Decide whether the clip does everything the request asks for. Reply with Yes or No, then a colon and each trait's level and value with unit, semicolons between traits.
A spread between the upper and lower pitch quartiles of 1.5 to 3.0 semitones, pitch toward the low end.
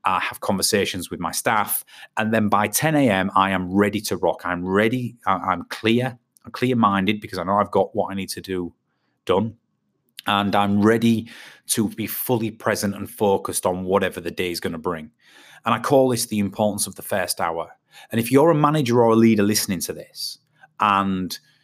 Yes: average, 2.7 semitones; low, 105 Hz